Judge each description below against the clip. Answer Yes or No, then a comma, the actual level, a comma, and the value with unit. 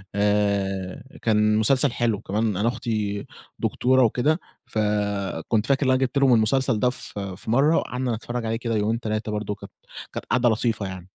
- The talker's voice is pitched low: Yes, low, 110 Hz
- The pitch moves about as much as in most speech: Yes, average, 3.1 semitones